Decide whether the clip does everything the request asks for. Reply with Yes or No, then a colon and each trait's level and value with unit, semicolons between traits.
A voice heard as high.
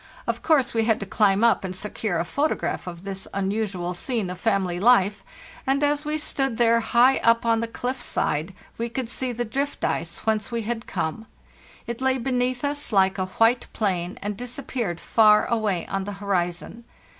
Yes: high, 225 Hz